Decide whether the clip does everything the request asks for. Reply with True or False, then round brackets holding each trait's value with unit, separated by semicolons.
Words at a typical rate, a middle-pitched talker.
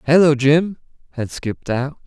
True (145 wpm; 145 Hz)